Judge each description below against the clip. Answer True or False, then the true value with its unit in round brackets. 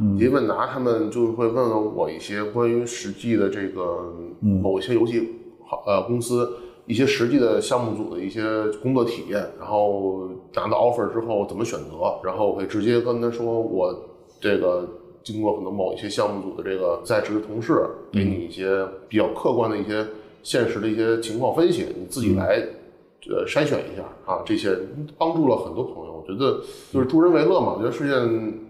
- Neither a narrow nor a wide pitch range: True (3.3 semitones)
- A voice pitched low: True (115 Hz)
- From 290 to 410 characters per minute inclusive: True (300 characters per minute)